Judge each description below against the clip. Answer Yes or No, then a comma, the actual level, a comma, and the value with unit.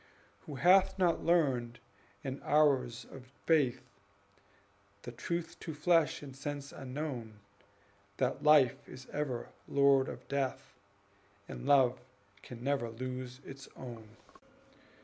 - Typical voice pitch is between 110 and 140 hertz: Yes, low, 135 Hz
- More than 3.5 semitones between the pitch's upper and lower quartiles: No, average, 2.8 semitones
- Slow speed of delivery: Yes, slow, 115 wpm